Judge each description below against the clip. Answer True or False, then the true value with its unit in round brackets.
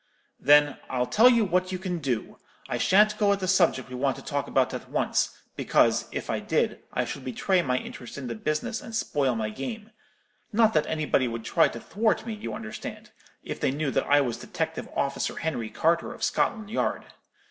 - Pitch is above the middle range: False (155 Hz)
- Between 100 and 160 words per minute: False (205 wpm)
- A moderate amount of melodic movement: False (8.0 semitones)